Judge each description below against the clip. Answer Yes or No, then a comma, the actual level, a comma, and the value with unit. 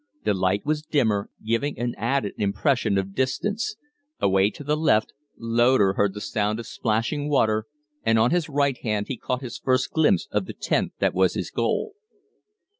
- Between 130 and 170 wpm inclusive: No, average, 180 wpm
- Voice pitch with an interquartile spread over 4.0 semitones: Yes, average, 5.2 semitones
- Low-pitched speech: Yes, low, 115 Hz